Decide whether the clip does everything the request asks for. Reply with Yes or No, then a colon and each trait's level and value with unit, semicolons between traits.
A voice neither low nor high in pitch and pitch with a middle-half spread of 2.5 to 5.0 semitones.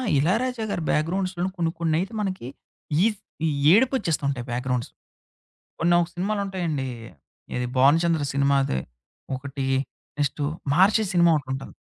No: medium, 165 Hz; wide, 5.4 semitones